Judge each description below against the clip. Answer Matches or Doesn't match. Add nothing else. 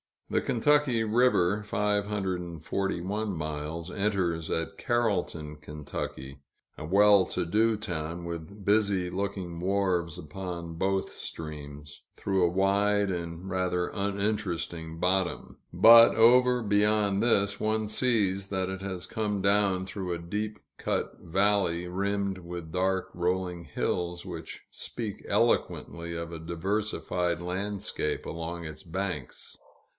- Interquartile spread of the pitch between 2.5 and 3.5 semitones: Matches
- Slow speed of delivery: Matches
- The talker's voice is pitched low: Matches